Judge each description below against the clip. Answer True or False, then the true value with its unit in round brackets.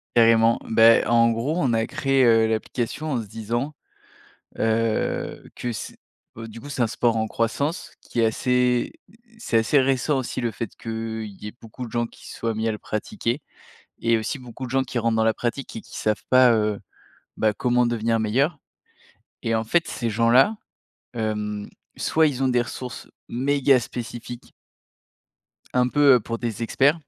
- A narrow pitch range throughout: True (2.3 semitones)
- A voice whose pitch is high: False (115 Hz)